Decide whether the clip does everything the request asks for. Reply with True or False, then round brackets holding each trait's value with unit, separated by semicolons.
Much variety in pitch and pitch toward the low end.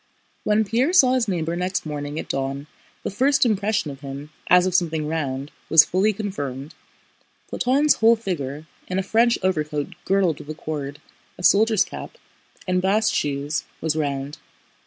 False (6.3 semitones; 175 Hz)